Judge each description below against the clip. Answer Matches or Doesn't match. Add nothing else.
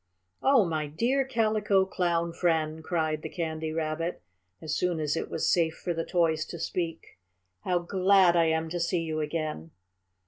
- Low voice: Doesn't match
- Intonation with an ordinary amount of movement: Doesn't match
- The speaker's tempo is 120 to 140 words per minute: Doesn't match